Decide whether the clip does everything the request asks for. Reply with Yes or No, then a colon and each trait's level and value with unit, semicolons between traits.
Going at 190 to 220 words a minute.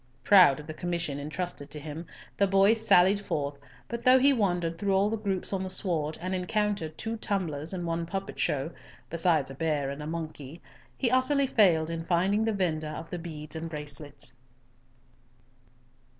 No: average, 175 wpm